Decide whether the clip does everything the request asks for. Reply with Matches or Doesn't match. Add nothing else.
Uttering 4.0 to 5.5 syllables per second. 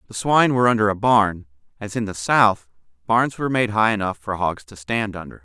Doesn't match